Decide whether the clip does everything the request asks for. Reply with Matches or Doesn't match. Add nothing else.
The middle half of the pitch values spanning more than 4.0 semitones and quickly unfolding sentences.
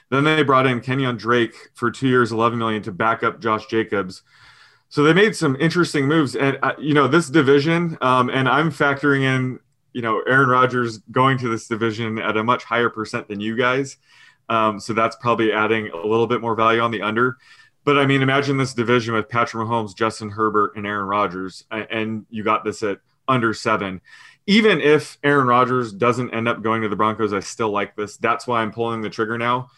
Doesn't match